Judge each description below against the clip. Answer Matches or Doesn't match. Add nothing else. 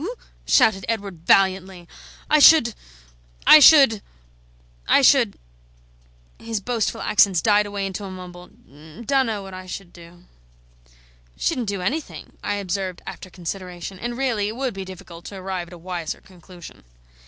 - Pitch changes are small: Doesn't match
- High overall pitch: Matches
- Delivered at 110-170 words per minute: Matches